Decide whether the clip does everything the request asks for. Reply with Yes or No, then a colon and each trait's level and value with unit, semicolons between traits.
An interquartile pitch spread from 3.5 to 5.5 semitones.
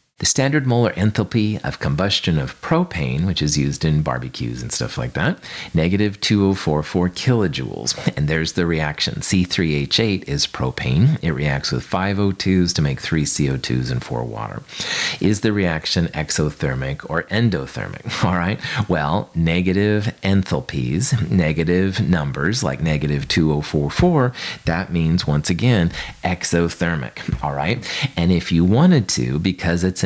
Yes: average, 4.9 semitones